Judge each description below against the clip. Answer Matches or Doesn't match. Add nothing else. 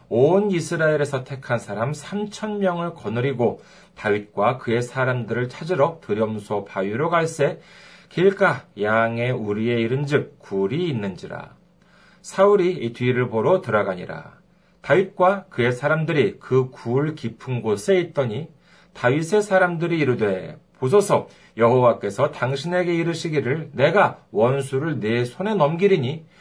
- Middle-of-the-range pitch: Matches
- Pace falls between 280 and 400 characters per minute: Matches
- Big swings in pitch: Matches